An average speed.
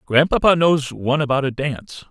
Yes: average, 170 wpm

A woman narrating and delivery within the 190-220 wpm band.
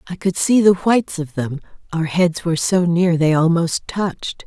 Yes: female; average, 200 wpm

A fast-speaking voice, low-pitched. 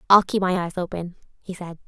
No: fast, 225 wpm; medium, 180 Hz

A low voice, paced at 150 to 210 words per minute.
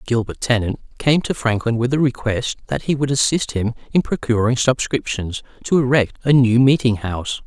Yes: low, 125 Hz; average, 175 wpm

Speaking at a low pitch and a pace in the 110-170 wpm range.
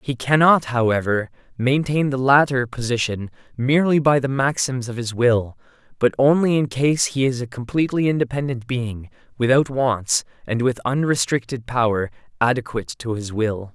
Yes: low, 125 Hz; average, 150 wpm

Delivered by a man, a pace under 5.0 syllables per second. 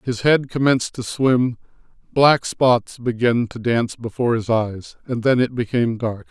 Yes: male; 4.7 syllables/s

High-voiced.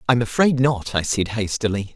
No: low, 115 Hz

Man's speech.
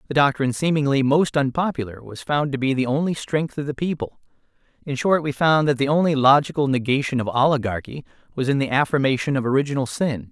Yes: male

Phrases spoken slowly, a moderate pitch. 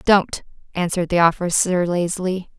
Yes: slow, 115 wpm; medium, 180 Hz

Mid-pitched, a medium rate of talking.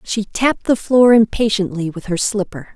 No: high, 210 Hz; average, 175 wpm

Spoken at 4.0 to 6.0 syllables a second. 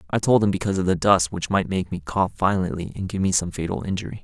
No: 6.5 syllables/s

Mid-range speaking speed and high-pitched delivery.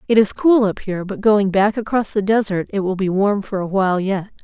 No: fast, 255 wpm; high, 200 Hz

